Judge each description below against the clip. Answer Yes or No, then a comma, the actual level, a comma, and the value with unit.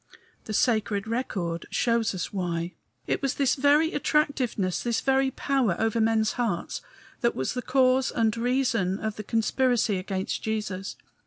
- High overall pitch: Yes, high, 225 Hz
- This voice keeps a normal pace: Yes, average, 150 wpm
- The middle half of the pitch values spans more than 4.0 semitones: Yes, average, 4.5 semitones